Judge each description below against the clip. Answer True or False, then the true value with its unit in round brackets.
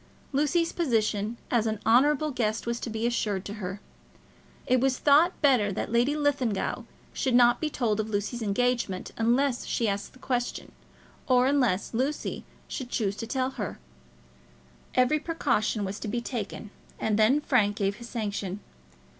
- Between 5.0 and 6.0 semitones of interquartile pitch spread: False (3.9 semitones)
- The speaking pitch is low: False (235 Hz)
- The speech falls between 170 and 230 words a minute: False (155 wpm)